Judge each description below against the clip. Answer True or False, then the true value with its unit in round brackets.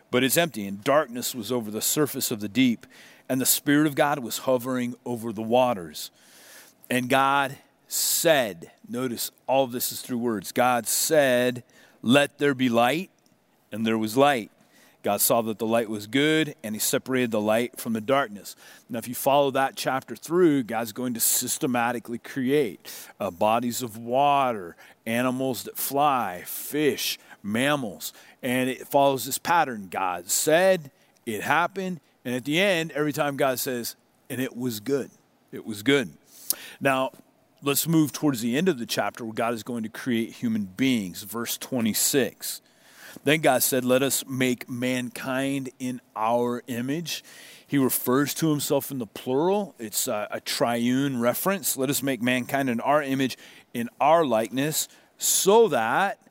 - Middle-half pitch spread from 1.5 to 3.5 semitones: True (3.0 semitones)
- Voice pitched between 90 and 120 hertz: False (130 Hz)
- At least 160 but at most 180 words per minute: True (165 wpm)